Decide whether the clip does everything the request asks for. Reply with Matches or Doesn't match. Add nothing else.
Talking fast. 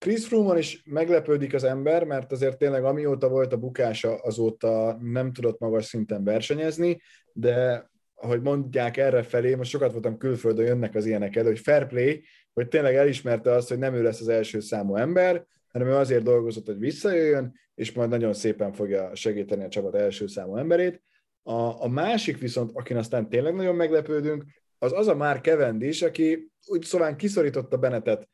Matches